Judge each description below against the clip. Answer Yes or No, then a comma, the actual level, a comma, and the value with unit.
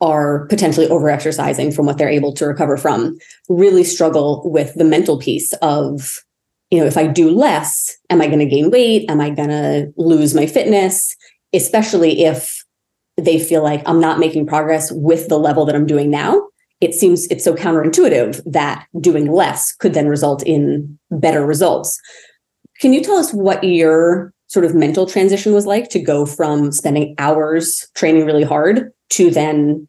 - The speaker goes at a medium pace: Yes, average, 175 wpm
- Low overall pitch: No, medium, 160 Hz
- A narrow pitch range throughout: No, average, 3.1 semitones